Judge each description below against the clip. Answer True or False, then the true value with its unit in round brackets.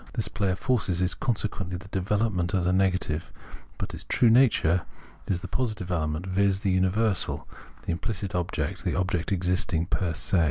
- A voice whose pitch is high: False (95 Hz)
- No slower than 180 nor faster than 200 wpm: False (170 wpm)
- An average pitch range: False (2.3 semitones)